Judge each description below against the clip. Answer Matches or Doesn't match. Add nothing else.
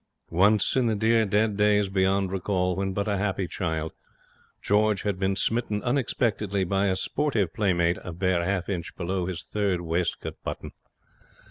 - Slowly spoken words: Doesn't match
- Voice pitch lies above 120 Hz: Doesn't match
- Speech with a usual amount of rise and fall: Doesn't match